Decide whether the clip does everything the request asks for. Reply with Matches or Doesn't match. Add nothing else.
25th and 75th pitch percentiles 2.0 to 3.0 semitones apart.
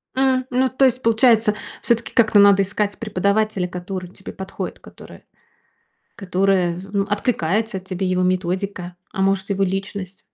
Matches